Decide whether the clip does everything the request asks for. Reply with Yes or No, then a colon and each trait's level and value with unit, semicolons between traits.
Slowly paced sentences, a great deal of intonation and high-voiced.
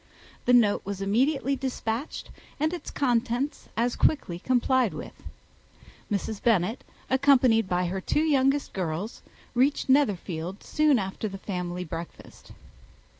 Yes: slow, 125 wpm; wide, 5.9 semitones; high, 230 Hz